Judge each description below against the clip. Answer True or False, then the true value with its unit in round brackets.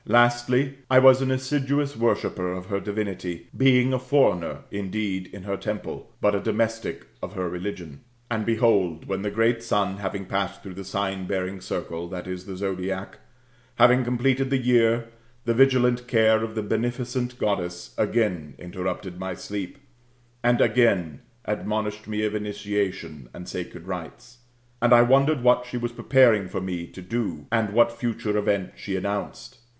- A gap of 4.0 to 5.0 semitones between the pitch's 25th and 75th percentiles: True (4.3 semitones)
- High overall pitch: False (105 Hz)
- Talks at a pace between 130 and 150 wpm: False (160 wpm)